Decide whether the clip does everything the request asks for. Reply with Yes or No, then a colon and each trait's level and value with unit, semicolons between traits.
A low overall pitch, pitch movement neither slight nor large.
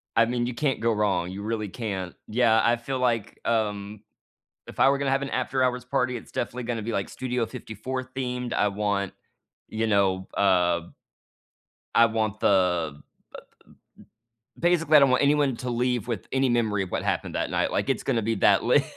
Yes: low, 115 Hz; average, 3.7 semitones